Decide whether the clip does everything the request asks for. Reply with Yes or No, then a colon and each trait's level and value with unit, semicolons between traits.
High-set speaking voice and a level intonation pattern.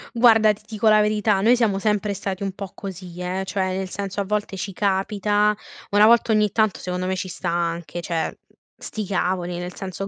Yes: high, 195 Hz; narrow, 2.3 semitones